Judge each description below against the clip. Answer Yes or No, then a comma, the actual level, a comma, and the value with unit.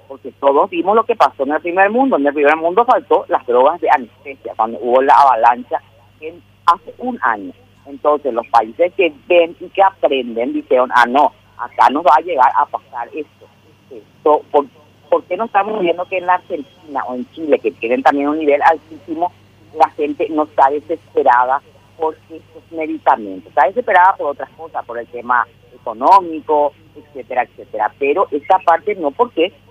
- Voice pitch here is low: No, medium, 160 Hz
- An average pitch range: No, wide, 6.3 semitones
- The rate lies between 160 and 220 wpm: Yes, average, 180 wpm